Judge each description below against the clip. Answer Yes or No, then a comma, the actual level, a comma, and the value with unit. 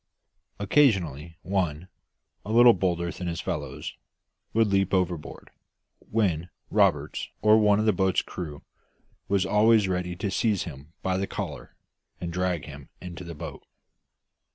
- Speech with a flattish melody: No, average, 3.2 semitones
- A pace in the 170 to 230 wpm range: No, average, 140 wpm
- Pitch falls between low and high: No, very low, 90 Hz